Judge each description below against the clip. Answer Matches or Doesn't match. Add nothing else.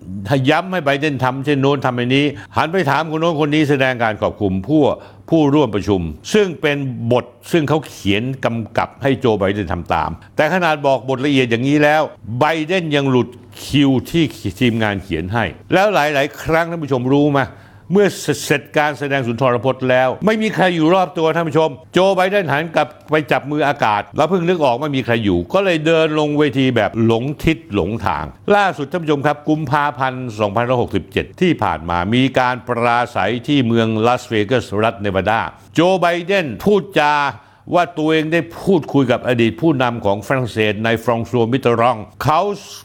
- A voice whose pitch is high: Doesn't match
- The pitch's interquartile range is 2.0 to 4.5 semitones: Doesn't match